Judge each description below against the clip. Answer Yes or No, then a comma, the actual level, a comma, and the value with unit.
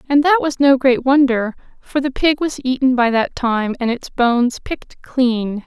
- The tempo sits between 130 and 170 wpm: No, average, 200 wpm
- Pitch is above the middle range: Yes, very high, 260 Hz